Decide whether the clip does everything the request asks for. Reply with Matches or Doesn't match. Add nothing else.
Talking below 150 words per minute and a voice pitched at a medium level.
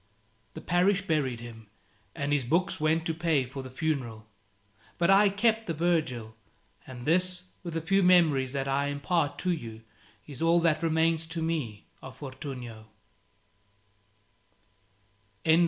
Matches